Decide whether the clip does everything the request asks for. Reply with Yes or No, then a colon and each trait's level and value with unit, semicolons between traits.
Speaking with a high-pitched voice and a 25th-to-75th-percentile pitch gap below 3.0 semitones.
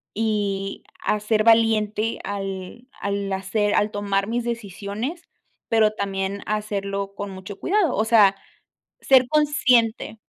Yes: high, 210 Hz; narrow, 2.4 semitones